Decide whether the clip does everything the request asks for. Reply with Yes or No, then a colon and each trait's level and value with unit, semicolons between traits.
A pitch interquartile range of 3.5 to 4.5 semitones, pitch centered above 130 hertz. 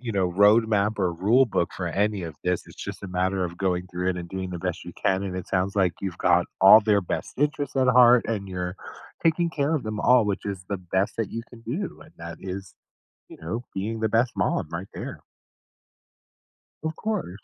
No: average, 4.1 semitones; low, 100 Hz